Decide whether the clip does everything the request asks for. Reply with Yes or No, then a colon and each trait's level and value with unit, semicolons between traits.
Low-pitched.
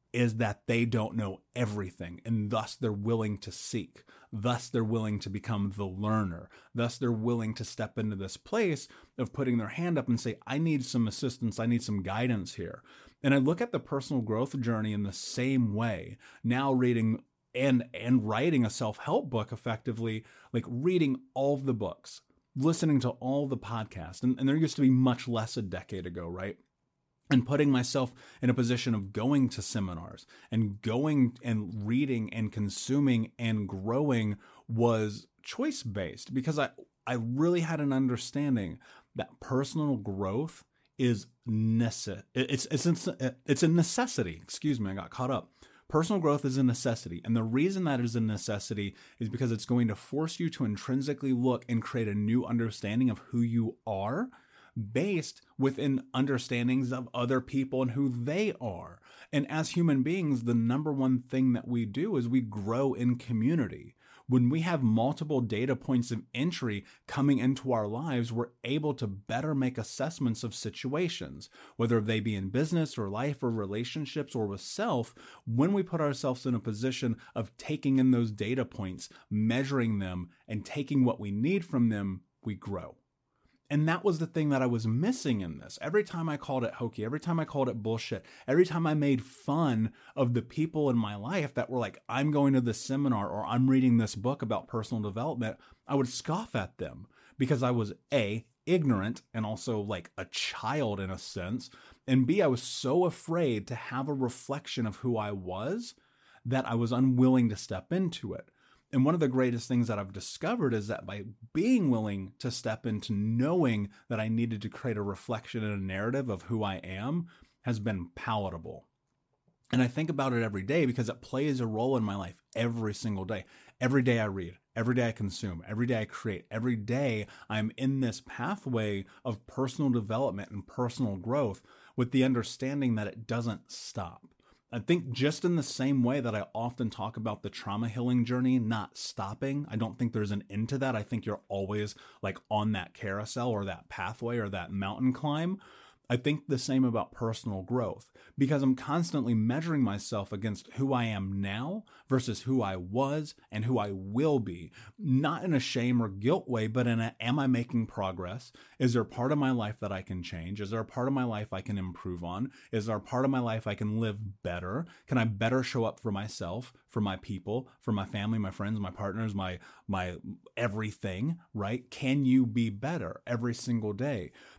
Yes: low, 120 Hz